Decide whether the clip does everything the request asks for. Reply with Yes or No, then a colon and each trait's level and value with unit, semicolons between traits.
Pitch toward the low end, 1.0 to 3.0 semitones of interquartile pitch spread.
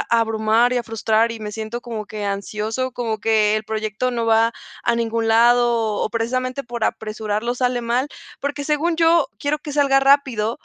No: high, 235 Hz; narrow, 2.6 semitones